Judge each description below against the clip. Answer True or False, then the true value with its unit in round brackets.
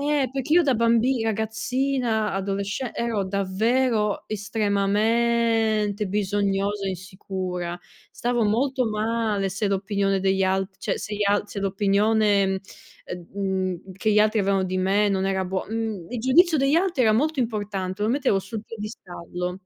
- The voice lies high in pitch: True (210 Hz)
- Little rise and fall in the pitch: False (3.0 semitones)